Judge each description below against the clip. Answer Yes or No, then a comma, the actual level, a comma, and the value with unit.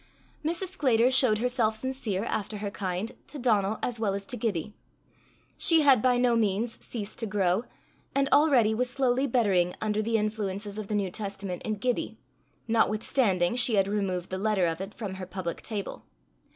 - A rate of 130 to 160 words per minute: No, average, 180 wpm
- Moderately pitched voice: No, high, 215 Hz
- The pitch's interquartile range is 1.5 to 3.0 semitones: No, average, 3.7 semitones